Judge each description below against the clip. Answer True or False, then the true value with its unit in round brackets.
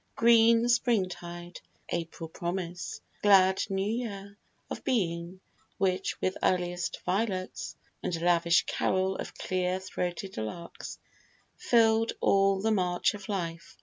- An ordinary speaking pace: False (115 wpm)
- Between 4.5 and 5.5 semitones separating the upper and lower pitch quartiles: False (2.6 semitones)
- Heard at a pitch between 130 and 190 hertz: True (185 Hz)